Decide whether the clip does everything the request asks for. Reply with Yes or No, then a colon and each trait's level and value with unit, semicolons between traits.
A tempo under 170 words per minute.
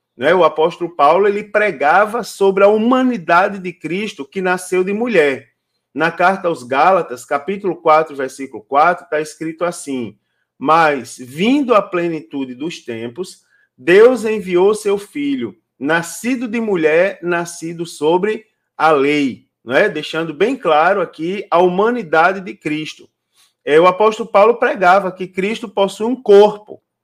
Yes: average, 135 wpm